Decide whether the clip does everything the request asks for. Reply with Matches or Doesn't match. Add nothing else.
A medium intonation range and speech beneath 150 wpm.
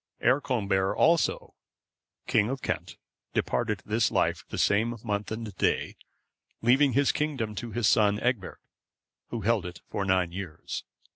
Matches